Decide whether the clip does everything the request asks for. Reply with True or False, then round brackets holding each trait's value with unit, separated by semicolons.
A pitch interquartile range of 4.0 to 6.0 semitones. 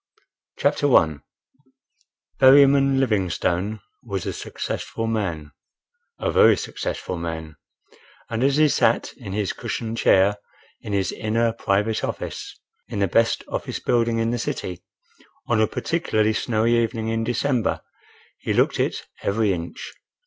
False (3.1 semitones)